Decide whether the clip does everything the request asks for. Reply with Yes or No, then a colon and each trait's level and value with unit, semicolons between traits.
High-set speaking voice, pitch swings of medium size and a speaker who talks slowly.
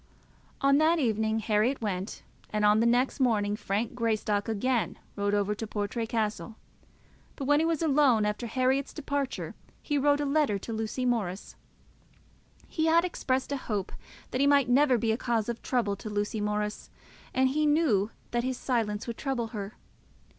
No: high, 235 Hz; average, 4.6 semitones; average, 175 wpm